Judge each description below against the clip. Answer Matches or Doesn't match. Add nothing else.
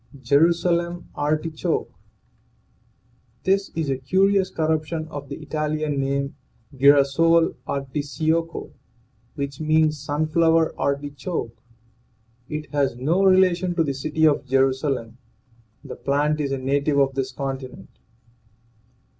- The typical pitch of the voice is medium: Matches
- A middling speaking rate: Doesn't match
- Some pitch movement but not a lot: Matches